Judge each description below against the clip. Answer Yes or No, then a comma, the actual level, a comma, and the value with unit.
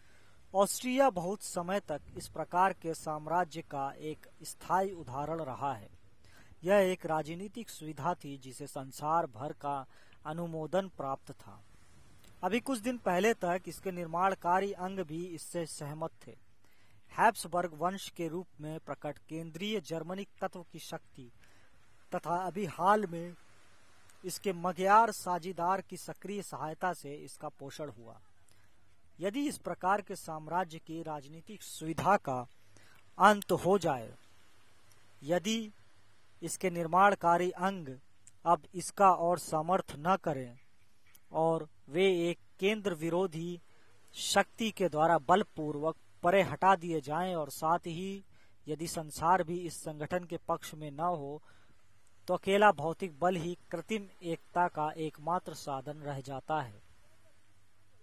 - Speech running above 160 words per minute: No, average, 130 wpm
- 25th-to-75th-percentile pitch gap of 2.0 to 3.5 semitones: No, average, 5.1 semitones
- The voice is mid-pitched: Yes, medium, 165 Hz